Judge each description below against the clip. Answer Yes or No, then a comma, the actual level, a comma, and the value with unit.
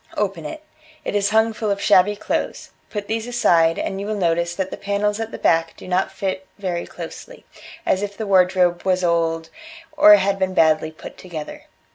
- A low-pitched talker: No, high, 190 Hz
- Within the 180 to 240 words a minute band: Yes, average, 195 wpm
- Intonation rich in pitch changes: No, average, 3.3 semitones